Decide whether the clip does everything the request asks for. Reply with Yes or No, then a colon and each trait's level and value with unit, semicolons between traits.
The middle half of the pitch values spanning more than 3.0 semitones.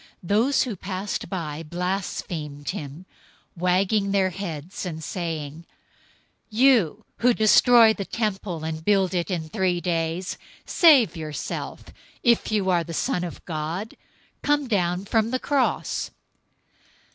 Yes: average, 4.5 semitones